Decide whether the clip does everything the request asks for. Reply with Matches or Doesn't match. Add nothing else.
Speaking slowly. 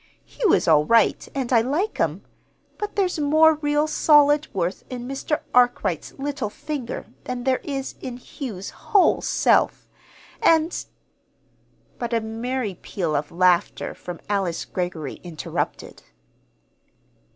Matches